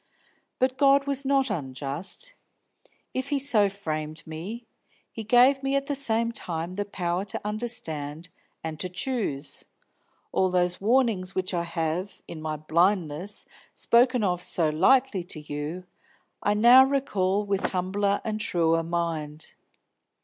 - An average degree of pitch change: No, wide, 6.4 semitones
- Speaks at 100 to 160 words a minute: Yes, average, 140 wpm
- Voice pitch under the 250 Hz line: Yes, high, 190 Hz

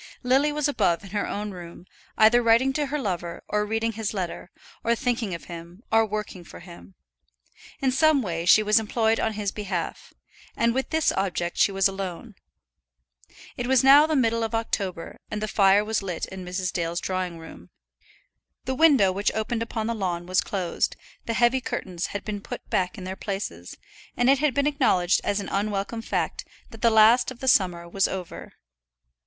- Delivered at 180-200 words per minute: Yes, average, 190 wpm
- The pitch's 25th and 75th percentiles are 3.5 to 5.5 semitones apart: Yes, average, 4.3 semitones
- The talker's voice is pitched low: No, high, 210 Hz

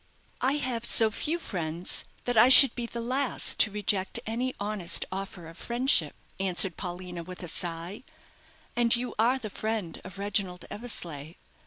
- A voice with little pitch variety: No, average, 5.0 semitones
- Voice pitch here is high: Yes, high, 205 Hz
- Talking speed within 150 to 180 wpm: Yes, average, 160 wpm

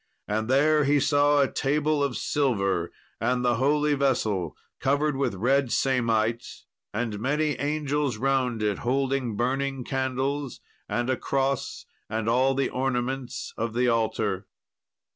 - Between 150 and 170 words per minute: No, slow, 135 wpm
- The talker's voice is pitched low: Yes, low, 130 Hz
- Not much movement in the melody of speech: No, average, 3.2 semitones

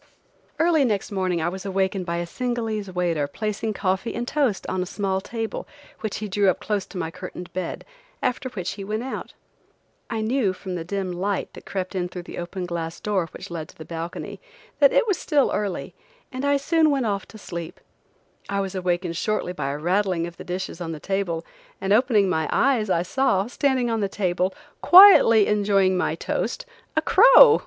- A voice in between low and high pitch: No, high, 195 Hz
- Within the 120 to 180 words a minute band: No, average, 200 wpm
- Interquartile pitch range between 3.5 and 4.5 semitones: Yes, average, 4.0 semitones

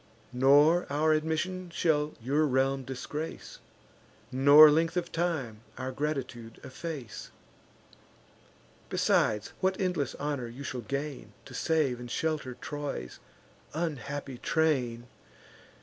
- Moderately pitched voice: Yes, medium, 145 Hz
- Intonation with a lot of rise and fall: No, average, 3.8 semitones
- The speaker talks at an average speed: No, slow, 105 wpm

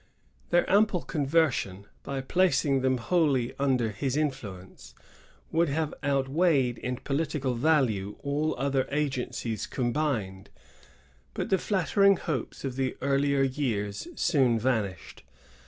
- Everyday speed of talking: No, slow, 115 wpm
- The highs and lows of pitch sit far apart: No, average, 4.1 semitones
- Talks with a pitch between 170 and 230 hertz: No, low, 135 Hz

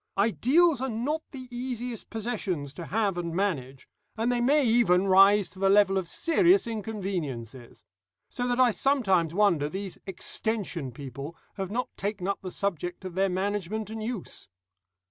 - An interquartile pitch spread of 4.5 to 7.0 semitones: Yes, average, 5.0 semitones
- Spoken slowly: No, average, 160 wpm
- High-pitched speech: Yes, high, 200 Hz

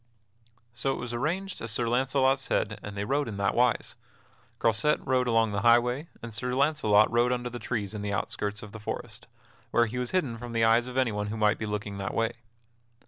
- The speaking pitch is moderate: No, low, 115 Hz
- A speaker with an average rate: No, fast, 215 wpm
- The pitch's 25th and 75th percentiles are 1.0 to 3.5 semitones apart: Yes, average, 2.9 semitones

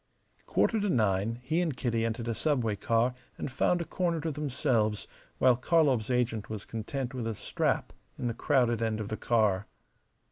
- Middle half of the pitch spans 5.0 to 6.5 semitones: No, average, 4.1 semitones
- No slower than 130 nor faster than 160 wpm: No, average, 180 wpm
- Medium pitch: No, low, 120 Hz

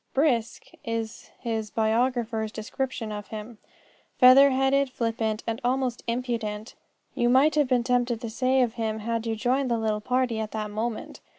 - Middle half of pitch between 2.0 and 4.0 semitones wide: Yes, narrow, 2.5 semitones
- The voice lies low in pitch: No, high, 235 Hz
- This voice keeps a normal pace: Yes, average, 165 wpm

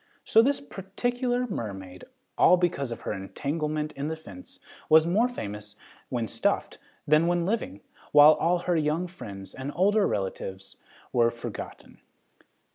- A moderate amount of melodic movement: No, wide, 8.2 semitones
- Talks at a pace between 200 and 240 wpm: No, average, 140 wpm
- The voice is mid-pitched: Yes, medium, 155 Hz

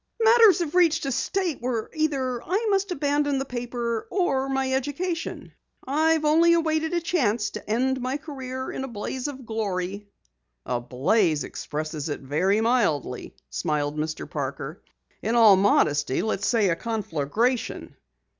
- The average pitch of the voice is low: No, very high, 250 Hz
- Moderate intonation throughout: No, wide, 7.5 semitones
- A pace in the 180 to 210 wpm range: No, average, 150 wpm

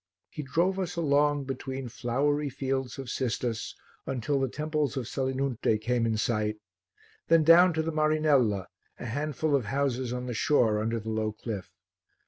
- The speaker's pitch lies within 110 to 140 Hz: Yes, low, 135 Hz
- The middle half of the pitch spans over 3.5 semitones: Yes, average, 4.1 semitones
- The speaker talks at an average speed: Yes, average, 160 wpm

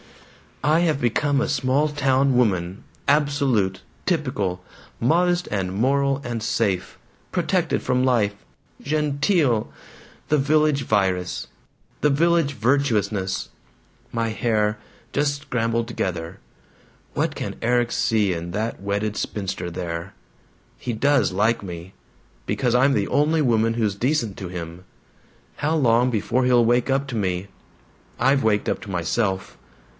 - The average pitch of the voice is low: Yes, low, 120 Hz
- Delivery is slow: Yes, slow, 130 wpm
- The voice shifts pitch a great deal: Yes, wide, 5.8 semitones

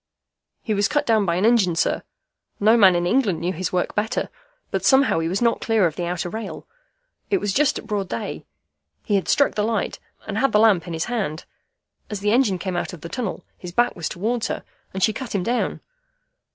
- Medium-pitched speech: No, high, 205 Hz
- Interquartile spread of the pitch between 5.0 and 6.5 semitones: No, average, 4.4 semitones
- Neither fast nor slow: No, fast, 225 wpm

